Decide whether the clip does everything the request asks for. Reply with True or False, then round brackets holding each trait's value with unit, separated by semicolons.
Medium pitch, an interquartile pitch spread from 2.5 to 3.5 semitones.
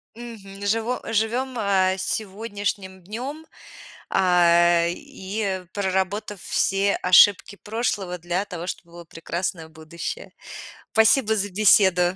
False (195 Hz; 3.2 semitones)